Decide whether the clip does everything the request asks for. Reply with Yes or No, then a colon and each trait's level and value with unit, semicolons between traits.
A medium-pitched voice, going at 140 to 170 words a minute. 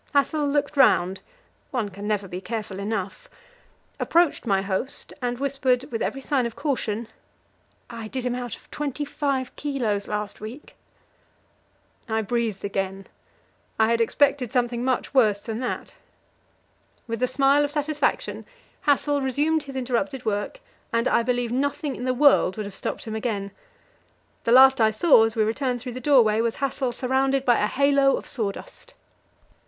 No: high, 245 Hz; average, 160 wpm